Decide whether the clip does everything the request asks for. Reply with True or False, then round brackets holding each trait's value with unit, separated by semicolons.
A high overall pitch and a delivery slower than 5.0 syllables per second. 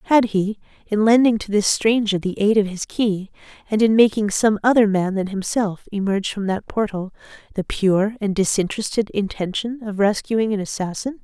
False (210 Hz; 5.1 syllables/s)